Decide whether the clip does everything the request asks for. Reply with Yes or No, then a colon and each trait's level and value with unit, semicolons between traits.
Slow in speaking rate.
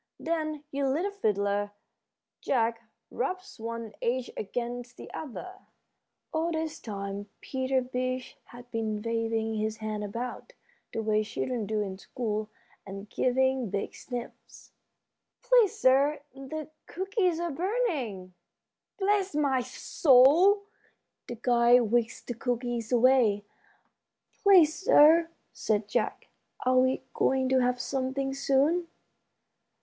Yes: slow, 115 wpm